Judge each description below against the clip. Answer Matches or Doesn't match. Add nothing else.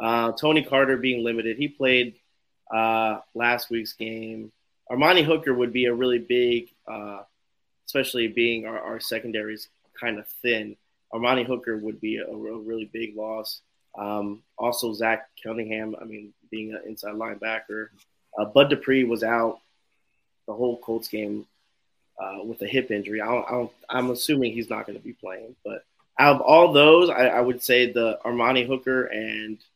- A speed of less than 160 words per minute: Doesn't match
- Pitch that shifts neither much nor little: Doesn't match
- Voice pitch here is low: Matches